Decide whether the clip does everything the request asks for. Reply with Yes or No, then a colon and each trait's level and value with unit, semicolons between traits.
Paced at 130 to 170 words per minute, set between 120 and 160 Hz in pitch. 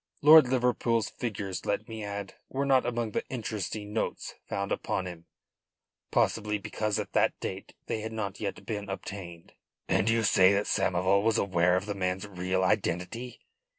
No: average, 165 wpm; low, 105 Hz